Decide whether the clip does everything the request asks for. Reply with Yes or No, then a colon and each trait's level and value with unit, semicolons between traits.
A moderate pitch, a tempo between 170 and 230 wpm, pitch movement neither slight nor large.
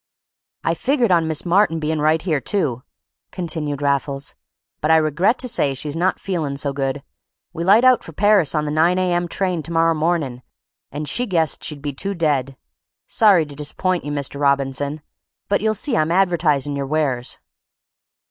Yes: medium, 155 Hz; average, 180 wpm; average, 4.1 semitones